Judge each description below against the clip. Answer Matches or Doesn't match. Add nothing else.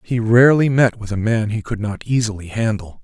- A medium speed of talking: Doesn't match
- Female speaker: Doesn't match